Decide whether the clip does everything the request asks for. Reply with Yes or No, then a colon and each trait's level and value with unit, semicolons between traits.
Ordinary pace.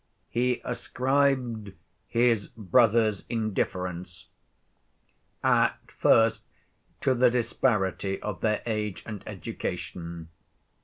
No: slow, 85 wpm